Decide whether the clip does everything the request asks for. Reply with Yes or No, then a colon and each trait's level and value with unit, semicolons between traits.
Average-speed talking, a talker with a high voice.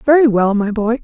No: fast, 235 wpm; high, 235 Hz